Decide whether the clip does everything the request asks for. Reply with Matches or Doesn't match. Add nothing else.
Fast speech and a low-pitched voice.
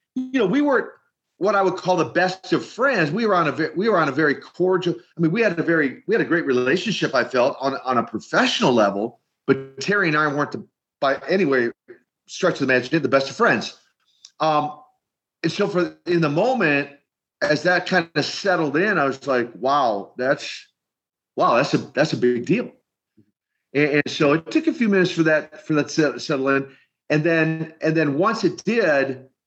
Doesn't match